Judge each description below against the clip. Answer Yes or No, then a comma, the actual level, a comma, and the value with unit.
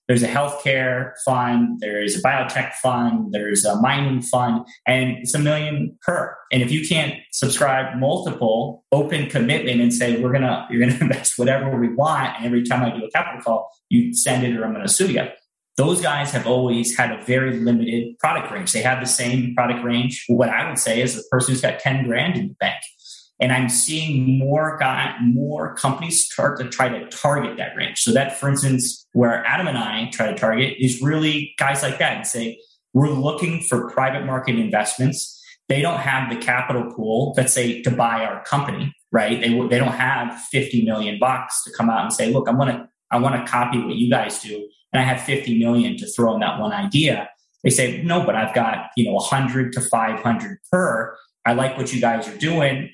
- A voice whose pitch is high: No, low, 125 Hz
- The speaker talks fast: Yes, fast, 215 wpm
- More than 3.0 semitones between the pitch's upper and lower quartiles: No, average, 2.7 semitones